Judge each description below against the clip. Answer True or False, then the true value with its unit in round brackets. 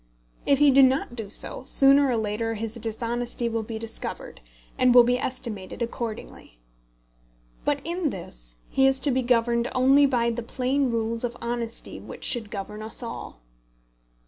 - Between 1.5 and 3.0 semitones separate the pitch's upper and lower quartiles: True (2.6 semitones)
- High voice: True (235 Hz)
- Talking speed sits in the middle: True (165 wpm)